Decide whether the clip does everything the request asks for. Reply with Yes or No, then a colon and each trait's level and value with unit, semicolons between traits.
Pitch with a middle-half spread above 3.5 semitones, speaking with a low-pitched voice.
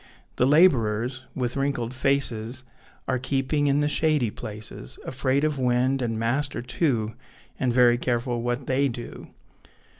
No: narrow, 2.6 semitones; low, 130 Hz